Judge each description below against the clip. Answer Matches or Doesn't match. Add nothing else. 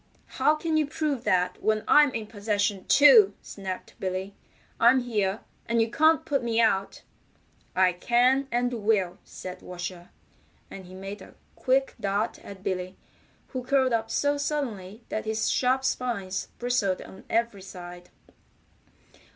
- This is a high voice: Matches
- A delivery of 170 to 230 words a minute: Doesn't match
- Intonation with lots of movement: Doesn't match